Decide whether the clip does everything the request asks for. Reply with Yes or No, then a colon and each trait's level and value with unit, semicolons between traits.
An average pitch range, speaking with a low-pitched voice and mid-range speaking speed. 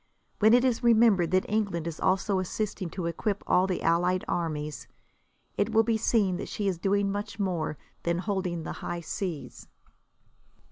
No: average, 3.5 semitones; high, 190 Hz; average, 170 wpm